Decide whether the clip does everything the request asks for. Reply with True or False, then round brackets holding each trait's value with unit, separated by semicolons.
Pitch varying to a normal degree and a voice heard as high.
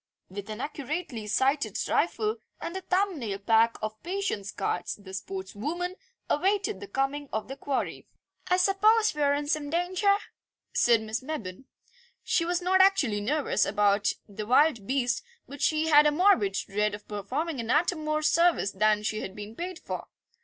False (8.4 semitones; 275 Hz)